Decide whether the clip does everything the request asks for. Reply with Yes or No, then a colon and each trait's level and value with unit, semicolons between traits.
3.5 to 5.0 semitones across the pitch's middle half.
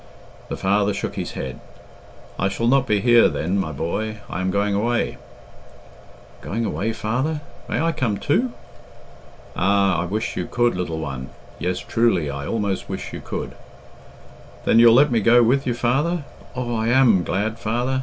Yes: average, 3.9 semitones